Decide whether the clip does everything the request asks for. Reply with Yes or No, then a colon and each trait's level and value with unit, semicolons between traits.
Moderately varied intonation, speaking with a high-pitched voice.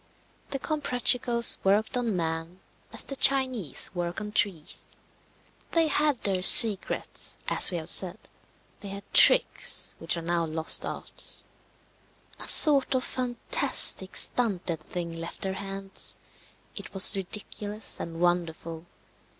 No: wide, 6.0 semitones; high, 195 Hz